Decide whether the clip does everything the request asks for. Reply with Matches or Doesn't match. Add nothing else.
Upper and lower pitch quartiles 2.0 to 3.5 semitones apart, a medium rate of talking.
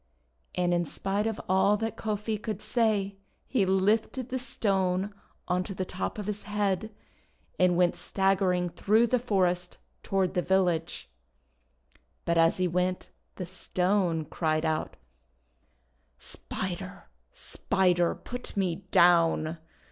Doesn't match